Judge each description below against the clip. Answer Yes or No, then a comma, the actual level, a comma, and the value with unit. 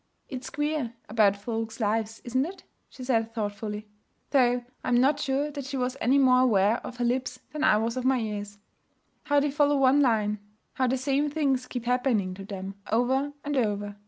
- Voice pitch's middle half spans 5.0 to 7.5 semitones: No, average, 3.8 semitones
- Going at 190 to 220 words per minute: Yes, average, 195 wpm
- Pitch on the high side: Yes, very high, 250 Hz